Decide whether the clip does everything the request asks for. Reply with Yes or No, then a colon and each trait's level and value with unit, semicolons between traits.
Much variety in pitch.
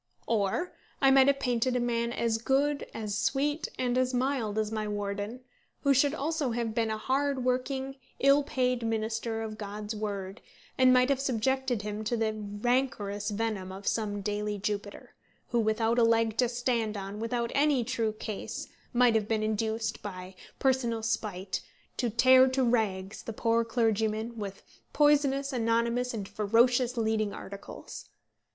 No: average, 3.2 semitones